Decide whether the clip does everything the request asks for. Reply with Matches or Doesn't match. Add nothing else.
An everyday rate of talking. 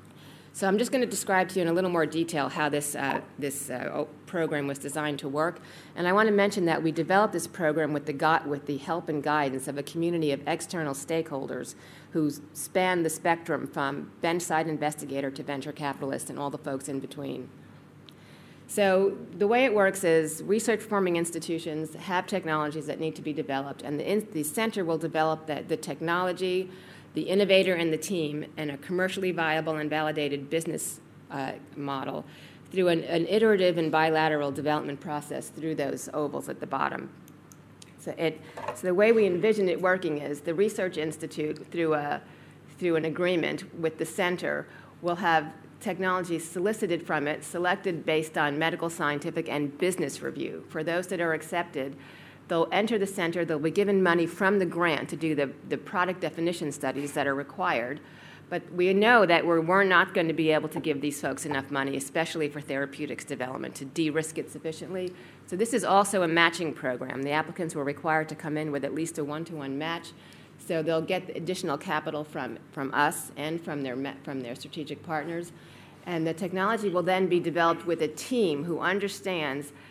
Matches